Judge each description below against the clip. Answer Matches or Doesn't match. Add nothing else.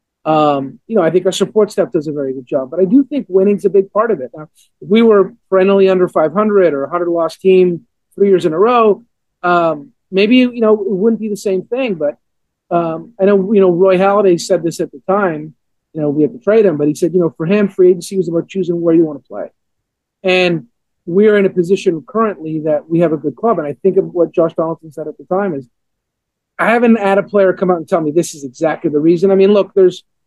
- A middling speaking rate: Doesn't match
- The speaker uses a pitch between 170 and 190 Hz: Matches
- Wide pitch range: Doesn't match